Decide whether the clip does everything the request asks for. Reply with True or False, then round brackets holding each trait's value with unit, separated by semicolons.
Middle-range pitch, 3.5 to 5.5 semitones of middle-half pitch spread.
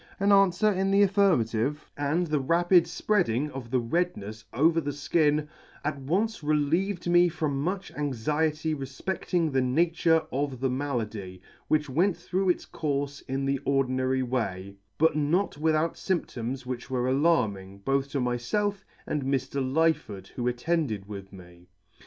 True (145 Hz; 4.9 semitones)